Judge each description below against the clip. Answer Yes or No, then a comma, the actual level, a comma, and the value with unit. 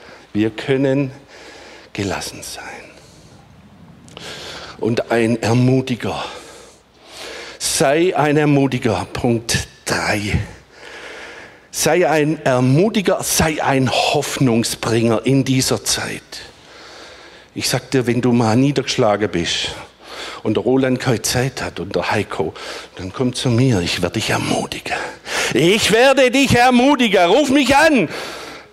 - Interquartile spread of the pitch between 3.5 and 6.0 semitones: Yes, average, 3.8 semitones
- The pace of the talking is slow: Yes, slow, 110 wpm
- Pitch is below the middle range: Yes, low, 130 Hz